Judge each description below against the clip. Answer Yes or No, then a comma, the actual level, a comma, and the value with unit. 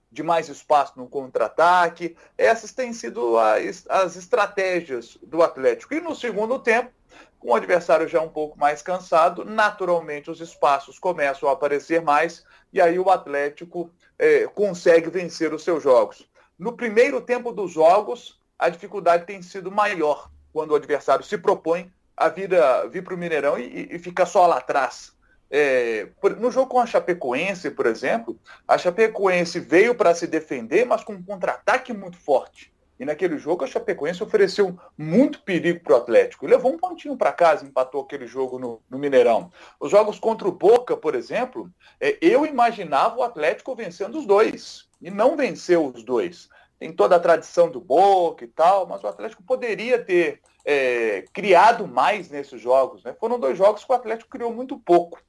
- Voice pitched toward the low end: No, medium, 185 Hz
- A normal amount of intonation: No, wide, 7.1 semitones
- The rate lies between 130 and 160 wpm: No, average, 170 wpm